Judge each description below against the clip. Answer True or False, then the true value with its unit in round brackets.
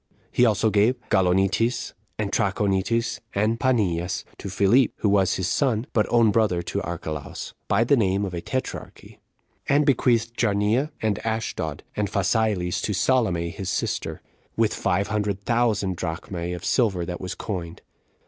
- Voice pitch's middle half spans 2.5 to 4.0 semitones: True (3.7 semitones)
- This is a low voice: True (100 Hz)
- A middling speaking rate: True (155 wpm)